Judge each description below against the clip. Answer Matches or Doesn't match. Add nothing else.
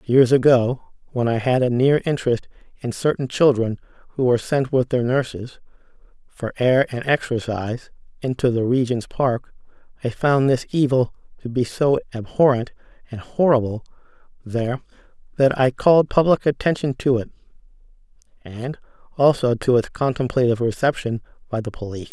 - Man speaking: Matches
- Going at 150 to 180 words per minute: Doesn't match